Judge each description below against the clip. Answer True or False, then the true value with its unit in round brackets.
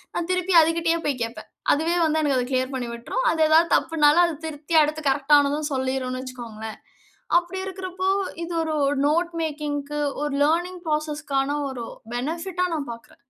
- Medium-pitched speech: False (300 Hz)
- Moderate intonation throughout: True (3.9 semitones)